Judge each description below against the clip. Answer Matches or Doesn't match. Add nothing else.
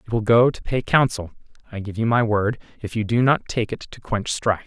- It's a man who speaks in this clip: Matches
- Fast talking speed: Matches